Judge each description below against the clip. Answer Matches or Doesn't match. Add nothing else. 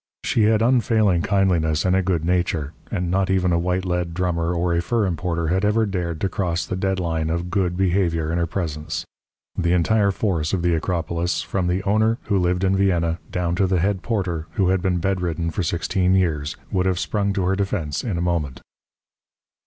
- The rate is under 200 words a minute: Doesn't match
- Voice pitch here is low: Matches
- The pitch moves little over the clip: Matches